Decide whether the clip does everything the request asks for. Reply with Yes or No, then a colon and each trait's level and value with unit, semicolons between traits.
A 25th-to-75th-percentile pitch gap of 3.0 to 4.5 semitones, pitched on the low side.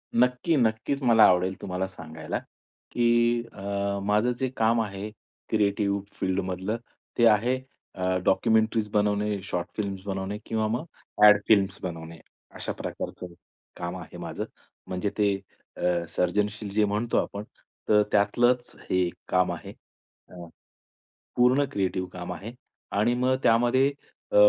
Yes: average, 3.5 semitones; low, 105 Hz